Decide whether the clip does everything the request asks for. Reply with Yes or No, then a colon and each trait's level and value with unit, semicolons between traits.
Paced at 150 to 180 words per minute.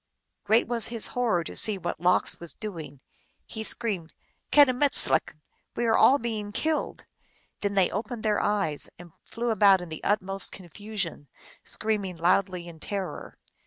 Yes: average, 160 wpm